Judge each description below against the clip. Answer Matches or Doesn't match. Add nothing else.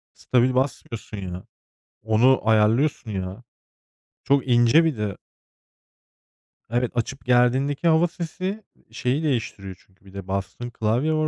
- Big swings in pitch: Doesn't match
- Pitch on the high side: Doesn't match